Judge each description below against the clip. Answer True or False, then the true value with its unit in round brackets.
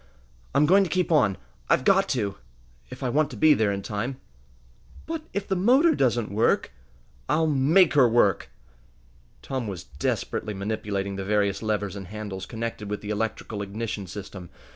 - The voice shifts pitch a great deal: True (6.5 semitones)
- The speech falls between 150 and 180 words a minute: True (165 wpm)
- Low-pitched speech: True (110 Hz)